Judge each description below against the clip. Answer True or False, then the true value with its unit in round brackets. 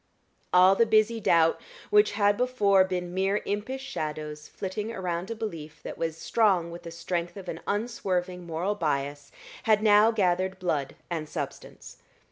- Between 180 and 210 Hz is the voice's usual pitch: True (185 Hz)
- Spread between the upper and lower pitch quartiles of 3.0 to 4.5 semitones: True (3.8 semitones)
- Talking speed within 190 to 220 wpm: False (155 wpm)